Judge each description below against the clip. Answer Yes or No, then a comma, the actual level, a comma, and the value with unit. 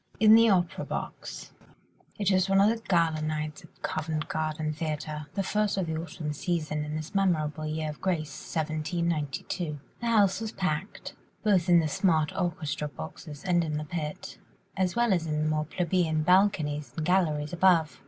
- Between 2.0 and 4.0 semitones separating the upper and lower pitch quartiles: Yes, average, 3.4 semitones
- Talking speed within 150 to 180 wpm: Yes, average, 175 wpm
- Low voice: No, medium, 160 Hz